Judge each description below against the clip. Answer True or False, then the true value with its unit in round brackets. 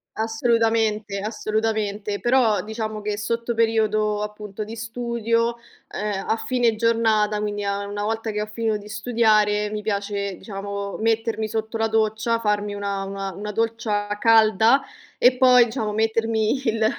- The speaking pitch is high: True (220 Hz)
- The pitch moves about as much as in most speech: False (1.5 semitones)